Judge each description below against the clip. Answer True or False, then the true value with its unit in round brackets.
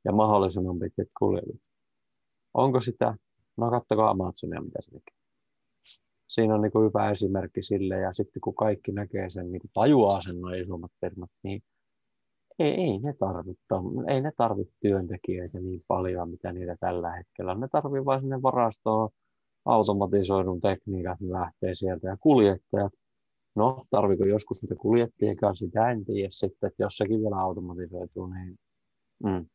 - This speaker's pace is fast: True (160 wpm)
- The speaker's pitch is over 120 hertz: False (100 Hz)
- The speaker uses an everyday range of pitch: True (3.1 semitones)